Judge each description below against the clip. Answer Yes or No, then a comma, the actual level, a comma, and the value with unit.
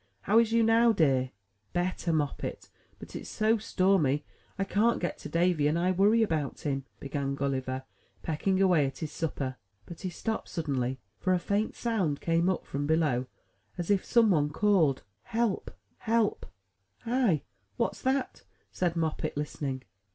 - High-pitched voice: No, medium, 170 Hz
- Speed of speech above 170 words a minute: No, average, 160 wpm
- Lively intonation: Yes, wide, 6.2 semitones